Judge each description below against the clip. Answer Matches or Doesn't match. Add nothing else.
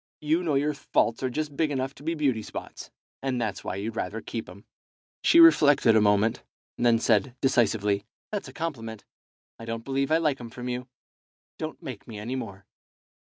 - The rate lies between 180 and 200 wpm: Matches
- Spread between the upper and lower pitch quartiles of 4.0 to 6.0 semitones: Matches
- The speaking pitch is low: Matches